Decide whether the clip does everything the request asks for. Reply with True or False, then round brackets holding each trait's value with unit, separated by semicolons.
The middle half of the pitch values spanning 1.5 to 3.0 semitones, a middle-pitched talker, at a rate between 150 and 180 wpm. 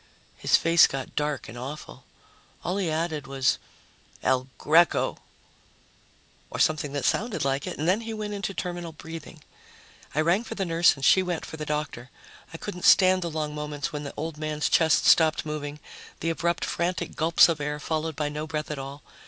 False (2.6 semitones; 155 Hz; 190 wpm)